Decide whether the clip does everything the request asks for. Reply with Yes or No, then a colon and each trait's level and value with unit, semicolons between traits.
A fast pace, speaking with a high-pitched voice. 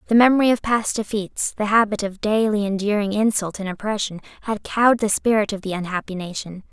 No: average, 190 wpm; high, 210 Hz